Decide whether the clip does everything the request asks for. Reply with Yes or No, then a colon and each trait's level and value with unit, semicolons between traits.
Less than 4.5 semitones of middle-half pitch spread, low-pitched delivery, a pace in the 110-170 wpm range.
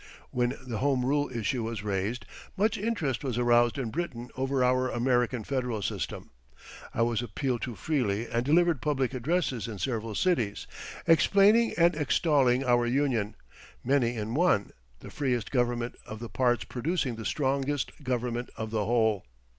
Yes: average, 3.5 semitones; low, 125 Hz; average, 155 wpm